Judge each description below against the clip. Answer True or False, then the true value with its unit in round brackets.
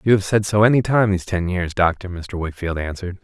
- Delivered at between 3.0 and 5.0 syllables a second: False (6.1 syllables/s)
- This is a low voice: True (95 Hz)